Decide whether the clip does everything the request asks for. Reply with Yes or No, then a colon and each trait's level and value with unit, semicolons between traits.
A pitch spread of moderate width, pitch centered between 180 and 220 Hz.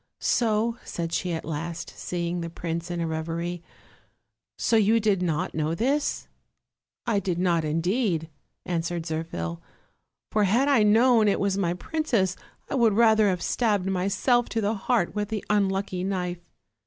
Yes: average, 4.3 semitones; high, 190 Hz